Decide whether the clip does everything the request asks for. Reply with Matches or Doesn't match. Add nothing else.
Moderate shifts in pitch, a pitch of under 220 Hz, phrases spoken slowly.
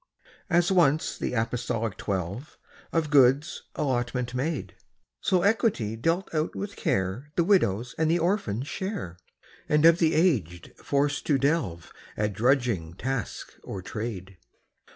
Doesn't match